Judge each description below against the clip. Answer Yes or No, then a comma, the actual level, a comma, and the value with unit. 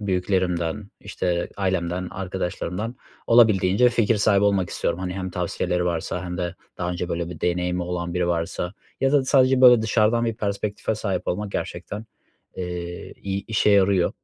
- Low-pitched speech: Yes, very low, 95 Hz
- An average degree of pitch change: Yes, average, 3.2 semitones